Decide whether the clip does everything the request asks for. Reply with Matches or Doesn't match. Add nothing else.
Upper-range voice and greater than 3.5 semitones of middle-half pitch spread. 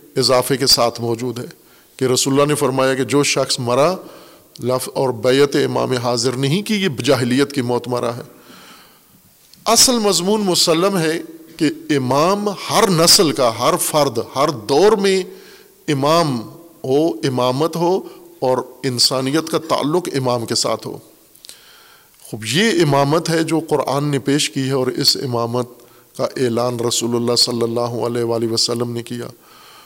Doesn't match